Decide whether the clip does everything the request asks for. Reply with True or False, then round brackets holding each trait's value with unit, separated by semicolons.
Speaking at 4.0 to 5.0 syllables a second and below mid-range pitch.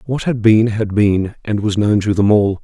True (4.6 syllables/s; 105 Hz)